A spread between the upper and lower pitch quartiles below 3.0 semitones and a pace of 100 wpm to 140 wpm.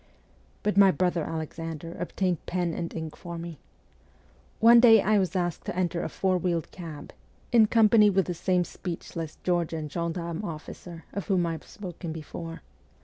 No: narrow, 2.4 semitones; average, 165 wpm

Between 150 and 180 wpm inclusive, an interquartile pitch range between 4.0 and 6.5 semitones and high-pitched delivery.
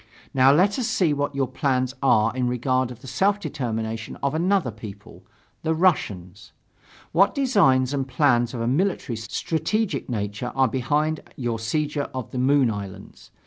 No: average, 160 wpm; average, 4.9 semitones; low, 130 Hz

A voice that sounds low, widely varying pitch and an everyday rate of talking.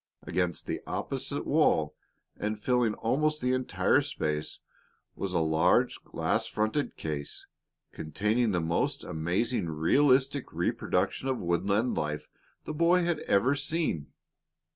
No: low, 105 Hz; wide, 7.7 semitones; slow, 120 wpm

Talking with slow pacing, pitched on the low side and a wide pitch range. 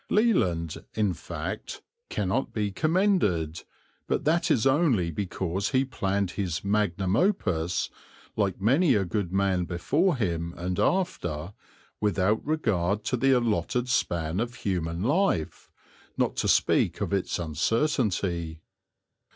Yes: slow, 125 wpm; low, 100 Hz; wide, 6.8 semitones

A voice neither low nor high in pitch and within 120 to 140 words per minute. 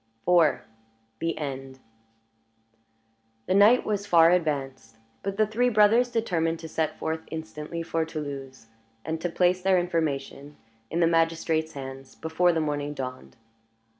Yes: medium, 160 Hz; slow, 135 wpm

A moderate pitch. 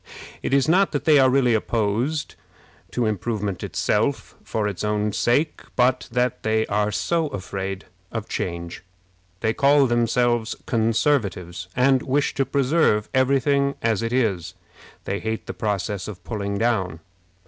No: low, 115 Hz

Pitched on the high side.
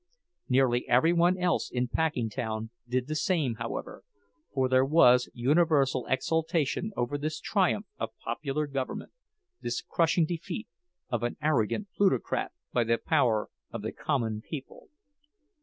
No: low, 135 Hz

